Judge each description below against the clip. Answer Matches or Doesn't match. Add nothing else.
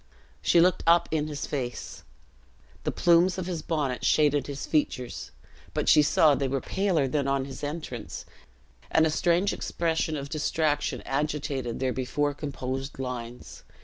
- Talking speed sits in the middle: Matches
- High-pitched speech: Doesn't match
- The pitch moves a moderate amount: Matches